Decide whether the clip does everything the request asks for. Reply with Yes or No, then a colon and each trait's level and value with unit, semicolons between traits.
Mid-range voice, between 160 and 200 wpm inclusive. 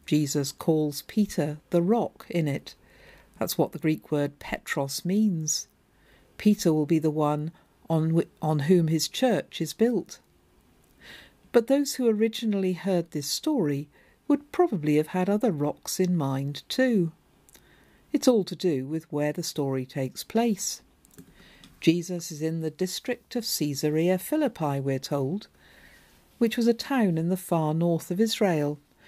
No: medium, 170 Hz; average, 150 wpm